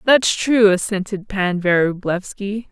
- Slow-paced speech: Yes, slow, 110 wpm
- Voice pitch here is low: No, high, 200 Hz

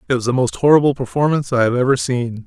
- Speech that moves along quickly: Yes, fast, 245 wpm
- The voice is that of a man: Yes, male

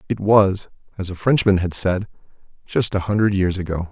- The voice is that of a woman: No, male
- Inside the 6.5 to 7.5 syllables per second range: No, 5.2 syllables/s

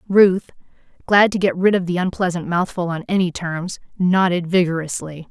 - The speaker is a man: No, female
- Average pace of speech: Yes, average, 160 wpm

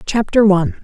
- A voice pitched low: No, high, 205 Hz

